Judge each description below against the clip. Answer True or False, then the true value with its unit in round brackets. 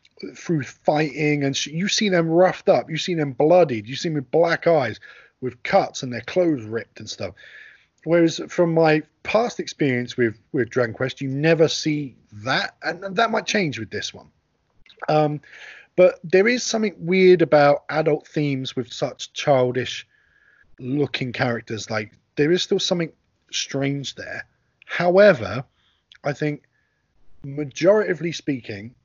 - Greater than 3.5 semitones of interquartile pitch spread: True (5.0 semitones)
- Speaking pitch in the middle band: True (150 Hz)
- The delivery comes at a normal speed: True (150 wpm)